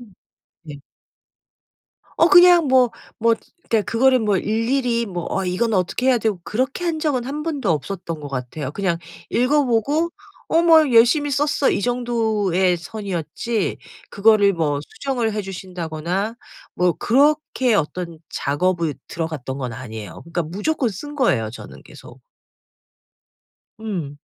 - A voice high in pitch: Yes, high, 215 Hz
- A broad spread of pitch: Yes, wide, 7.3 semitones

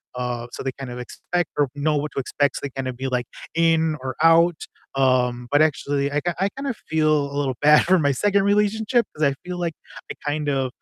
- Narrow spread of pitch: No, average, 3.9 semitones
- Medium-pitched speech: Yes, medium, 145 Hz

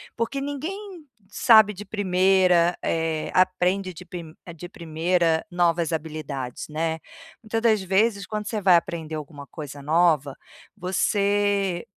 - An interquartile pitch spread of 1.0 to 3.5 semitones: No, average, 4.0 semitones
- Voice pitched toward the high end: No, medium, 180 Hz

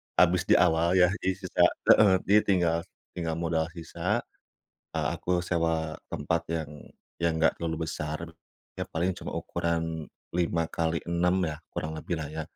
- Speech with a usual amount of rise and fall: No, narrow, 1.4 semitones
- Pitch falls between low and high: No, very low, 85 Hz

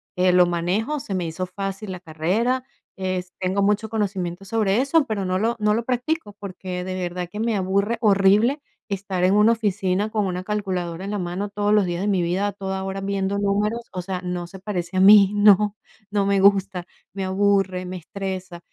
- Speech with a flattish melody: Yes, narrow, 2.2 semitones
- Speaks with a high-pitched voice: Yes, high, 195 Hz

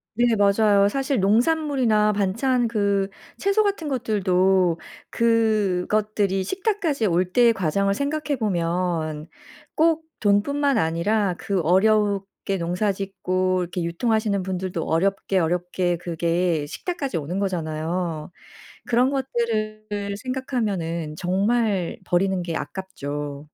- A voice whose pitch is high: Yes, high, 200 Hz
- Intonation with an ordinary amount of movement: Yes, average, 4.4 semitones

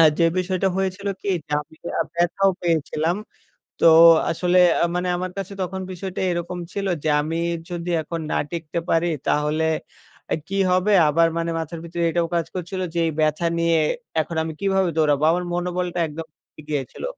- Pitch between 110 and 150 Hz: No, medium, 170 Hz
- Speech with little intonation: Yes, narrow, 2.1 semitones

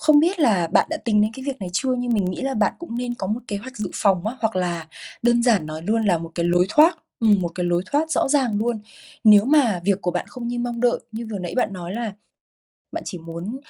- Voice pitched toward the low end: No, high, 220 Hz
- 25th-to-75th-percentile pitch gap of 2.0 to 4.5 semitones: No, average, 5.1 semitones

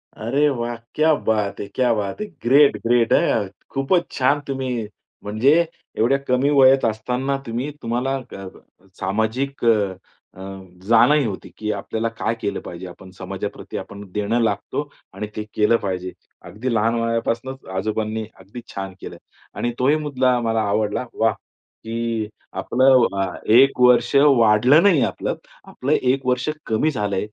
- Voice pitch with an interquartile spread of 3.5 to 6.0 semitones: Yes, average, 3.8 semitones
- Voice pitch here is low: Yes, low, 115 Hz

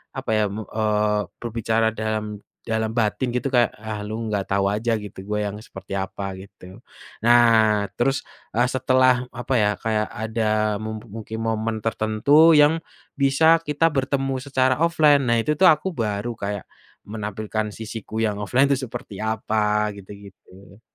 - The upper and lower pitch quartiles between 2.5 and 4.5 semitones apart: Yes, average, 3.2 semitones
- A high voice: No, low, 110 Hz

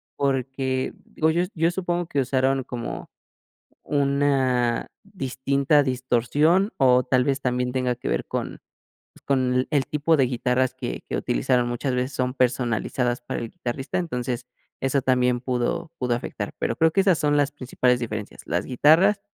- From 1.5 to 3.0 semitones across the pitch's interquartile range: Yes, narrow, 2.6 semitones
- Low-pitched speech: Yes, low, 130 Hz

